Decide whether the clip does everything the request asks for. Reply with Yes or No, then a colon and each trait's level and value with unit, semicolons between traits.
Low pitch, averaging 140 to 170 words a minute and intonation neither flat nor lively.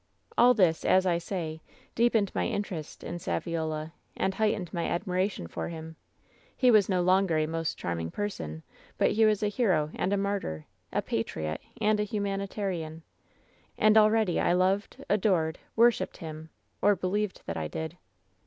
No: medium, 185 Hz; average, 160 wpm; average, 4.4 semitones